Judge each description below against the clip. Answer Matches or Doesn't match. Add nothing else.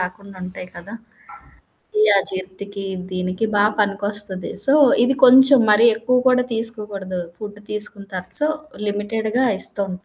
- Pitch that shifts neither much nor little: Matches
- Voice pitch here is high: Matches